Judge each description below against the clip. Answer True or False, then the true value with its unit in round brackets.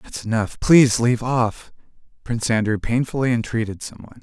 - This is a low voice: True (115 Hz)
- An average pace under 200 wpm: True (140 wpm)